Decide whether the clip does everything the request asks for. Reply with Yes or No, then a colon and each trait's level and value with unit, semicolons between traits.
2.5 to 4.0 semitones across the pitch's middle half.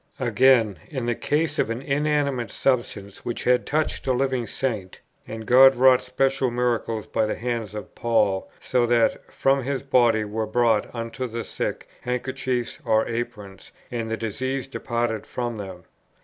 Yes: average, 2.8 semitones